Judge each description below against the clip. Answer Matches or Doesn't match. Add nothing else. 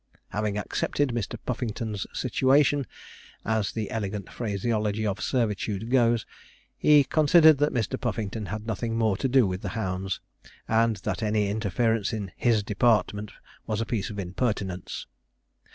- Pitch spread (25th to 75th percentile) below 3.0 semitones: Matches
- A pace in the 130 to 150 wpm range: Matches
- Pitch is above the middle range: Doesn't match